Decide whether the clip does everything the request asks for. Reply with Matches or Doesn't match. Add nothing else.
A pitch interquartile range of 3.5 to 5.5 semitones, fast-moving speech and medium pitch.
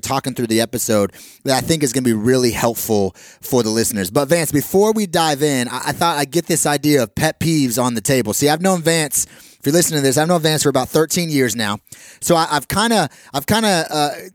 Matches